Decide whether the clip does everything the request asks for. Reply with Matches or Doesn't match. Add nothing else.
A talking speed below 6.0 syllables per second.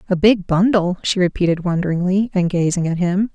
Matches